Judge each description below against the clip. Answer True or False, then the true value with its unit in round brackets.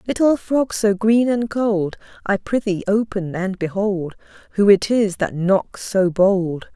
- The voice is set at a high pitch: True (200 Hz)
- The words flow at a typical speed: True (160 wpm)